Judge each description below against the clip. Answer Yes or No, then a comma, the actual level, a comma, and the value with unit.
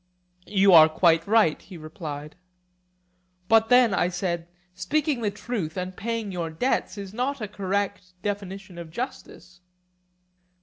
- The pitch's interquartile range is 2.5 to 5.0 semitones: Yes, average, 4.0 semitones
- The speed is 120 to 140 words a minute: Yes, slow, 135 wpm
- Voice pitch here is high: Yes, high, 195 Hz